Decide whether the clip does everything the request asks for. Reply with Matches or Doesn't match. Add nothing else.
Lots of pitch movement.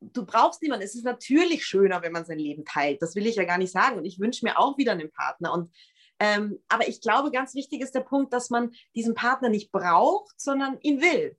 Matches